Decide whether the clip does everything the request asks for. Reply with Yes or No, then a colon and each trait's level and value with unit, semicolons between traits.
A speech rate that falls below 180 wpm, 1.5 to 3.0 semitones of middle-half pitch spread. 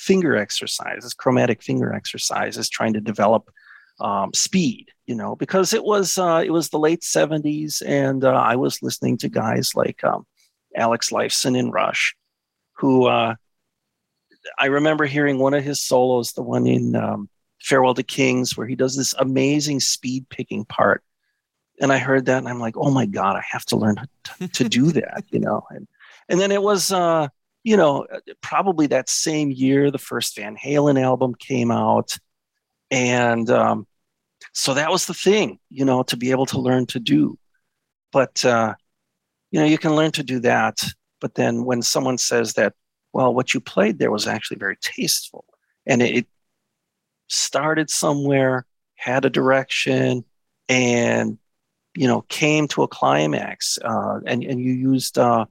No: average, 170 wpm; average, 3.6 semitones